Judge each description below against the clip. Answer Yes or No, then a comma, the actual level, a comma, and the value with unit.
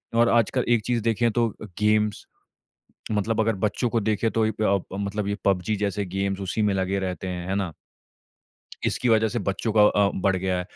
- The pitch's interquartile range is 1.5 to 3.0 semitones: Yes, narrow, 2.4 semitones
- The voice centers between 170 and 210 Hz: No, low, 105 Hz